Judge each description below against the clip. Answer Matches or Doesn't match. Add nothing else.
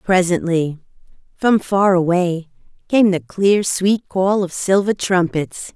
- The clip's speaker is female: Matches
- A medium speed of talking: Doesn't match